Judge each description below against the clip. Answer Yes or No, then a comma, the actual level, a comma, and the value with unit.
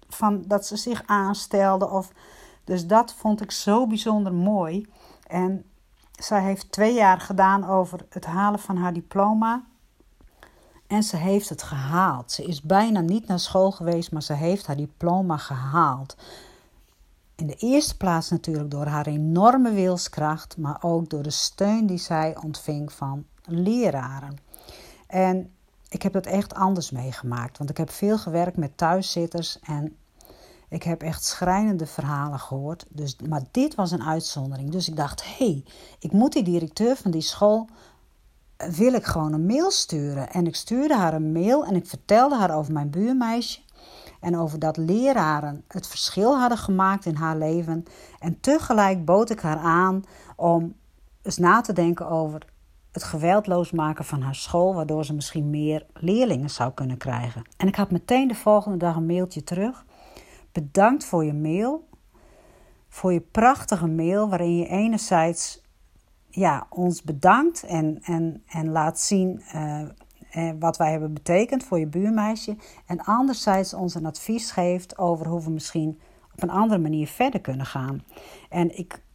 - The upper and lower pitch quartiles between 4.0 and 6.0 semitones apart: Yes, average, 4.4 semitones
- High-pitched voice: No, medium, 175 Hz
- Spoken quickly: No, average, 160 wpm